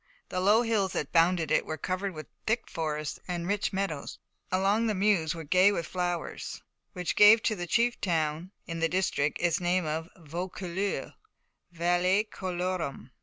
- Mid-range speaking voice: Yes, medium, 180 Hz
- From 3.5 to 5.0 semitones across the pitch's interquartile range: No, average, 3.0 semitones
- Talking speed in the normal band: Yes, average, 170 wpm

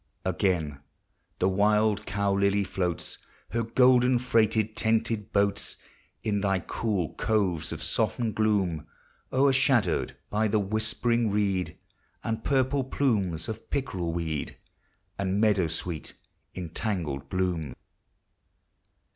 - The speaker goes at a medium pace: No, slow, 110 wpm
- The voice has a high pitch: No, low, 105 Hz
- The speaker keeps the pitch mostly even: No, average, 3.6 semitones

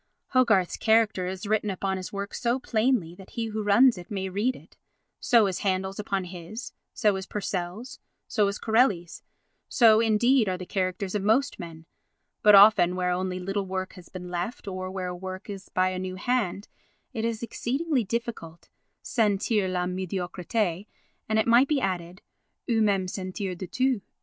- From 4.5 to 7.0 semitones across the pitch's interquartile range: No, average, 3.3 semitones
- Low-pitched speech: No, high, 195 Hz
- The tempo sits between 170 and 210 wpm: Yes, average, 175 wpm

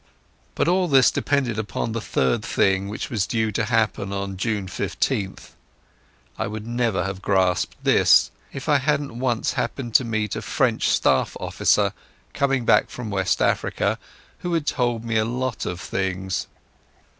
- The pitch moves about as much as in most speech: Yes, average, 4.3 semitones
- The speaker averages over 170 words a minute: No, average, 160 wpm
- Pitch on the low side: Yes, low, 110 Hz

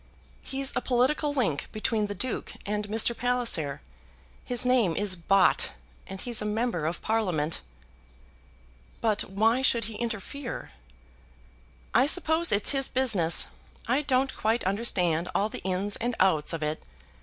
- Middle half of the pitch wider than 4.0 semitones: Yes, average, 4.8 semitones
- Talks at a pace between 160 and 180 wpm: No, average, 145 wpm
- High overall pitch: Yes, high, 220 Hz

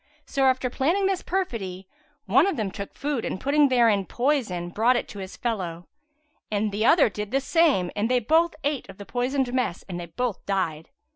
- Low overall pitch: No, high, 240 Hz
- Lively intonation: Yes, wide, 5.9 semitones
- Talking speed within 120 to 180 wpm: No, average, 195 wpm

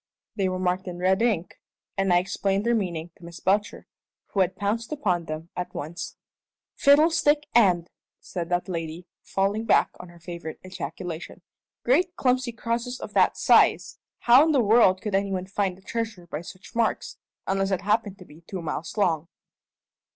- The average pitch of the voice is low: No, high, 190 Hz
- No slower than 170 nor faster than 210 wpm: Yes, average, 175 wpm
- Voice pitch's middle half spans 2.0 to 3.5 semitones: No, average, 4.4 semitones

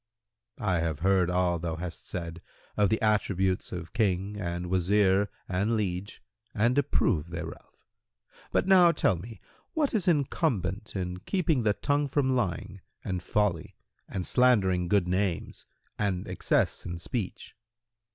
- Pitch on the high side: No, very low, 95 Hz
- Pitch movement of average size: Yes, average, 4.2 semitones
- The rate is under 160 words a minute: Yes, average, 140 wpm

